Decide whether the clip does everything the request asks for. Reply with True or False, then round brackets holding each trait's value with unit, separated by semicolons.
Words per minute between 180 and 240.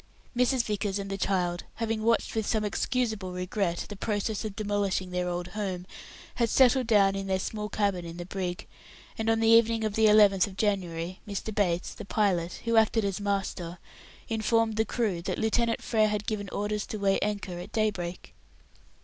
True (185 wpm)